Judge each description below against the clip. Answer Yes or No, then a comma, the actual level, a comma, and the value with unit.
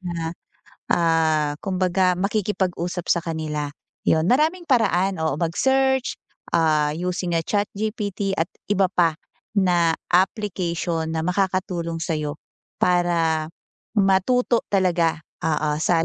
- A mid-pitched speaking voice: Yes, medium, 175 Hz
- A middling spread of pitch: Yes, average, 3.1 semitones